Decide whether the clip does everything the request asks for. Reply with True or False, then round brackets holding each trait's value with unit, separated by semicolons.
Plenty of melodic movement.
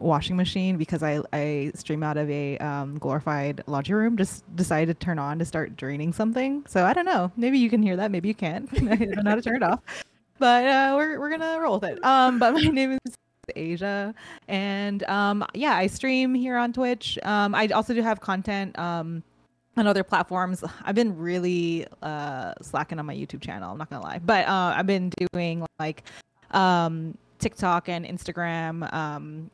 True (5.7 semitones)